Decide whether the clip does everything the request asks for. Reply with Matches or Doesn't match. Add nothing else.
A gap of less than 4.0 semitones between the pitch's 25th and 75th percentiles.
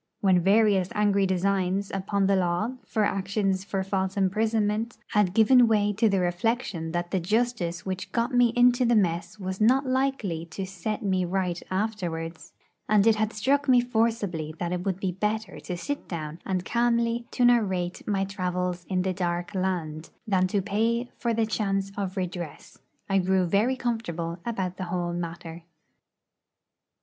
Matches